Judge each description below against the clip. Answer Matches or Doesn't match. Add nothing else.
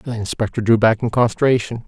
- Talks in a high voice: Doesn't match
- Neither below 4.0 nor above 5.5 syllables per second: Doesn't match